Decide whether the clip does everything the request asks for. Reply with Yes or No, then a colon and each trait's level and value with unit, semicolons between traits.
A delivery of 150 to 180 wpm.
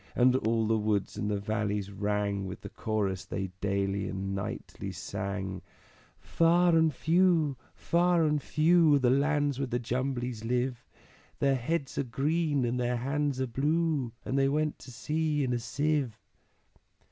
Yes: average, 160 wpm